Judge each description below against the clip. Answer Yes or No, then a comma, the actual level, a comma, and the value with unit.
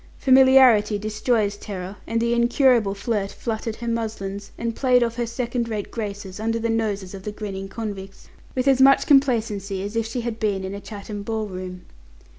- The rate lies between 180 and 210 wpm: Yes, average, 185 wpm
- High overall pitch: Yes, high, 220 Hz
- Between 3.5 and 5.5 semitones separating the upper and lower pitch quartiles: No, average, 2.8 semitones